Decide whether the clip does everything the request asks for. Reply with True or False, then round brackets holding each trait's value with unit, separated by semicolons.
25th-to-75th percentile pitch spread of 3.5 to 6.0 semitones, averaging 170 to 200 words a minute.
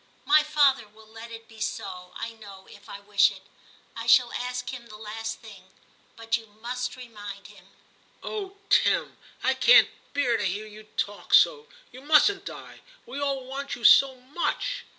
True (4.3 semitones; 180 wpm)